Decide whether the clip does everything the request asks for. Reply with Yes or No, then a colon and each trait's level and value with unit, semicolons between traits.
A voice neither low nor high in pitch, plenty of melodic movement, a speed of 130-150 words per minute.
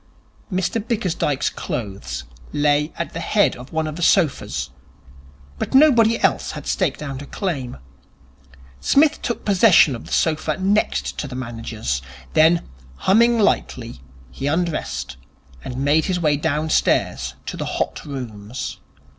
Yes: medium, 155 Hz; wide, 6.9 semitones; average, 140 wpm